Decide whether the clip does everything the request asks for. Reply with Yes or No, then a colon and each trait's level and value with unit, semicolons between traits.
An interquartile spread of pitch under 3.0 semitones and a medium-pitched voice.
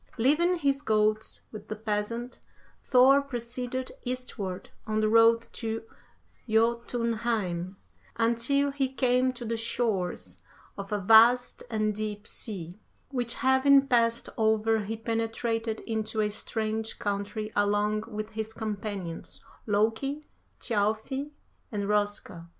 No: narrow, 2.5 semitones; high, 225 Hz